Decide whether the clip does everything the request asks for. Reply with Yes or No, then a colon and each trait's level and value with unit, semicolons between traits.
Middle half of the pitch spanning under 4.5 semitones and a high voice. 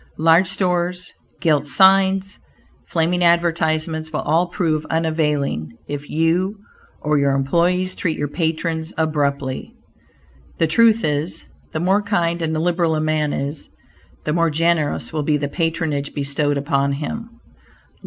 No: average, 2.9 semitones; medium, 160 Hz